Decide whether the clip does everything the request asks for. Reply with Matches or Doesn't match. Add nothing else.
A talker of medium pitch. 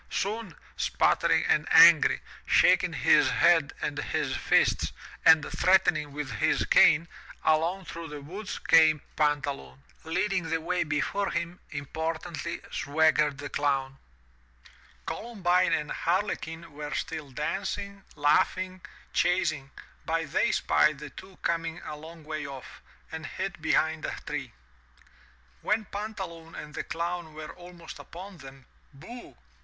Matches